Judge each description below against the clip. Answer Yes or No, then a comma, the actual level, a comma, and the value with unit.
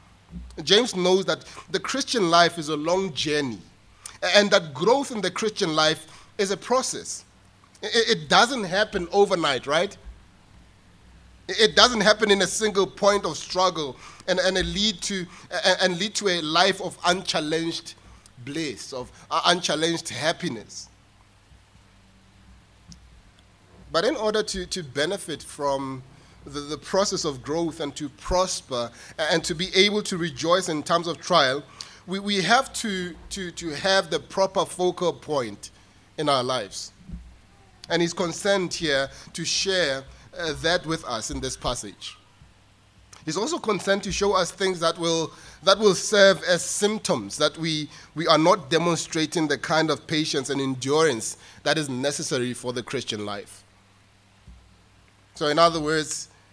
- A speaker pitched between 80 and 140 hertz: No, medium, 165 Hz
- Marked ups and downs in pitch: Yes, wide, 6.9 semitones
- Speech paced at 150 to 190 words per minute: No, average, 140 wpm